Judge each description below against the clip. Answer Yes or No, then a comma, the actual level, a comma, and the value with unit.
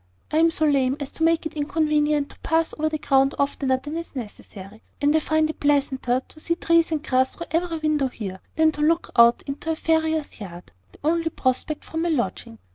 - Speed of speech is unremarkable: No, fast, 215 wpm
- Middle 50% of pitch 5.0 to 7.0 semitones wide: No, average, 3.3 semitones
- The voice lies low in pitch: No, very high, 300 Hz